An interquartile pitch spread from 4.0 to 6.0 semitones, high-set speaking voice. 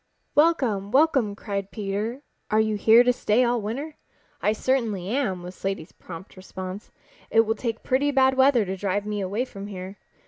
Yes: average, 4.4 semitones; high, 215 Hz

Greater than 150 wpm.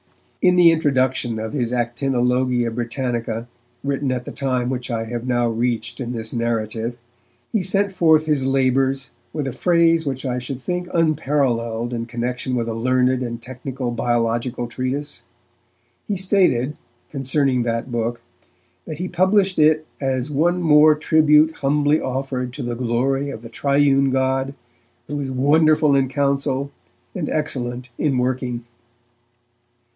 No: average, 145 wpm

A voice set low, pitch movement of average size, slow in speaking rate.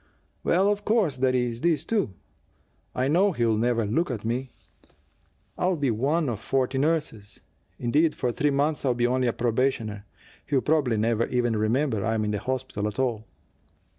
No: low, 125 Hz; average, 4.6 semitones; average, 165 wpm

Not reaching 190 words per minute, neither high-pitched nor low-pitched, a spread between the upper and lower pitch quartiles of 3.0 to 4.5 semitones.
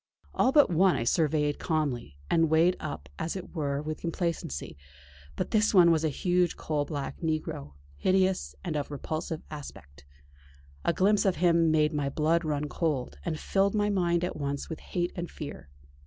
Yes: average, 175 wpm; medium, 160 Hz; average, 3.4 semitones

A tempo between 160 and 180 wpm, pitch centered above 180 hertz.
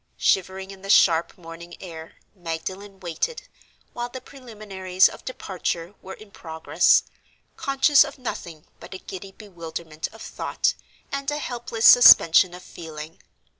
No: slow, 135 wpm; high, 190 Hz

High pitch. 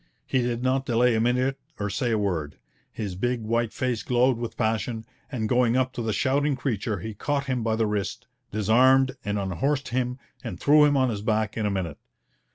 No: low, 120 Hz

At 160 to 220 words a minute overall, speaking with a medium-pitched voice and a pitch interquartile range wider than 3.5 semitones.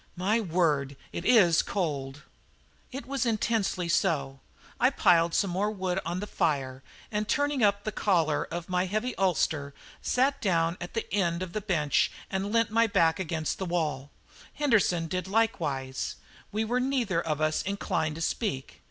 Yes: average, 165 wpm; medium, 180 Hz; average, 5.0 semitones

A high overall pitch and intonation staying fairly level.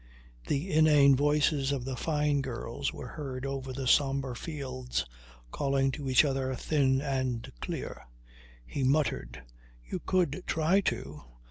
No: low, 135 Hz; narrow, 2.2 semitones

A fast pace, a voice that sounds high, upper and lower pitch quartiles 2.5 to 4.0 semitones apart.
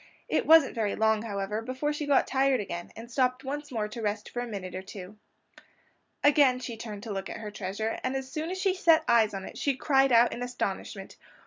No: fast, 225 wpm; high, 235 Hz; average, 4.4 semitones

